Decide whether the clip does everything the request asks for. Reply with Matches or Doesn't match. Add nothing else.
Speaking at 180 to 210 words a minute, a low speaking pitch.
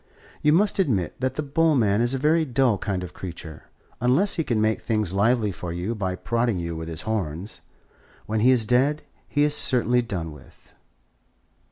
Matches